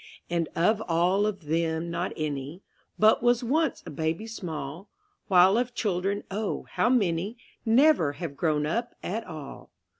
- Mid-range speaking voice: Yes, medium, 180 Hz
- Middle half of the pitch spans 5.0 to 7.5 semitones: Yes, wide, 5.4 semitones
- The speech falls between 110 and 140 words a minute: No, average, 150 wpm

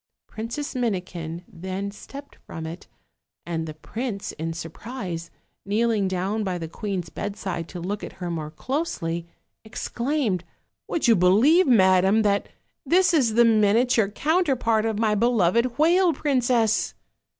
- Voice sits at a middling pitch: No, high, 210 Hz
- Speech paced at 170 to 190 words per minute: No, average, 140 wpm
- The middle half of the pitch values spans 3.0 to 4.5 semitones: No, average, 5.2 semitones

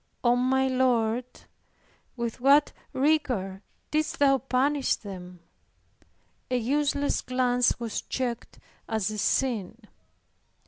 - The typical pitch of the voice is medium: No, very high, 250 Hz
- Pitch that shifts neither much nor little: Yes, average, 3.1 semitones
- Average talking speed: No, slow, 100 wpm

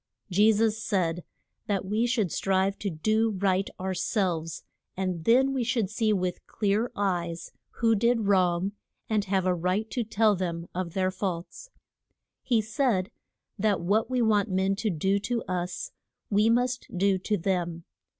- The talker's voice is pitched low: No, high, 200 Hz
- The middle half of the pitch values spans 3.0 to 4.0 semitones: Yes, average, 3.3 semitones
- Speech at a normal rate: Yes, average, 160 wpm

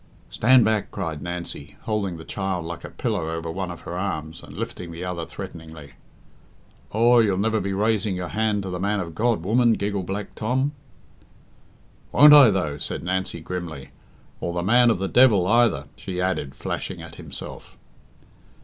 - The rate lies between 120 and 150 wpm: No, average, 175 wpm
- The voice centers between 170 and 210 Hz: No, very low, 95 Hz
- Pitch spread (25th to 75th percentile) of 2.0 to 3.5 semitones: No, average, 4.2 semitones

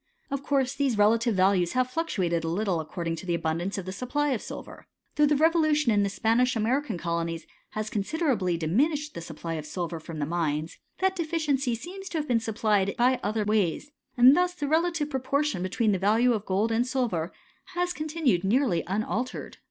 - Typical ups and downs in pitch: No, wide, 7.9 semitones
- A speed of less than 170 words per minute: No, average, 200 wpm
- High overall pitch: Yes, high, 225 Hz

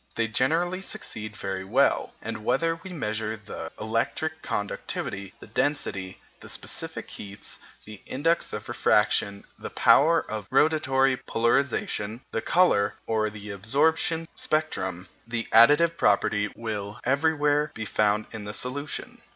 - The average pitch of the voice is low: Yes, low, 115 Hz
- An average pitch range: No, wide, 6.0 semitones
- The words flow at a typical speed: No, slow, 130 wpm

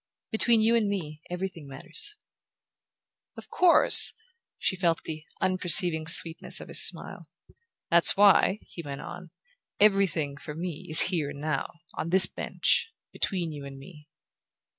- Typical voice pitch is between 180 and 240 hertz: No, medium, 170 Hz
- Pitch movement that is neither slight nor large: Yes, average, 3.9 semitones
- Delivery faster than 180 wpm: No, average, 140 wpm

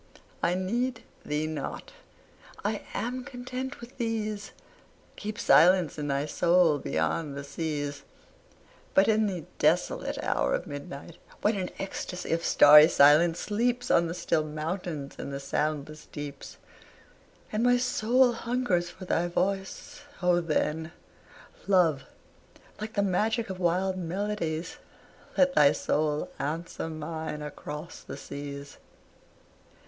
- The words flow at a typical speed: No, slow, 125 wpm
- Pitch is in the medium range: Yes, medium, 175 Hz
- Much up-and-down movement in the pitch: Yes, wide, 5.7 semitones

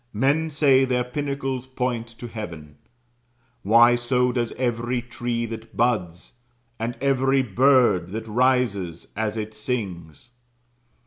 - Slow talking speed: Yes, slow, 120 wpm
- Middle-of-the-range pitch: No, low, 120 Hz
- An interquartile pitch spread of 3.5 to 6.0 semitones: No, average, 2.8 semitones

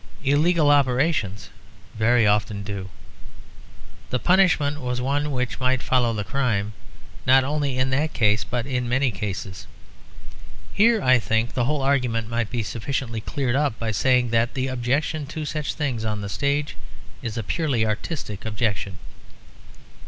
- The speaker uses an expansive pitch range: No, average, 4.3 semitones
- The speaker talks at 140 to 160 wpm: Yes, average, 150 wpm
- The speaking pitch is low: Yes, low, 125 Hz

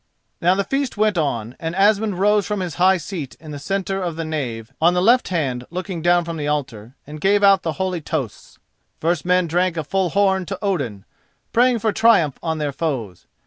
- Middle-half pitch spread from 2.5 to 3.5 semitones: No, average, 4.6 semitones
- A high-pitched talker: No, medium, 175 Hz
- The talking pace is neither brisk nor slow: No, fast, 210 wpm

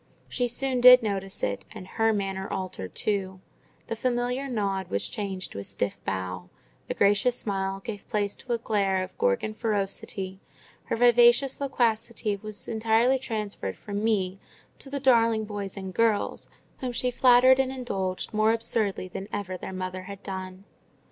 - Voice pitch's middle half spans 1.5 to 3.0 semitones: No, average, 3.8 semitones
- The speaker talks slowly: No, average, 160 wpm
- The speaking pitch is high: Yes, high, 210 Hz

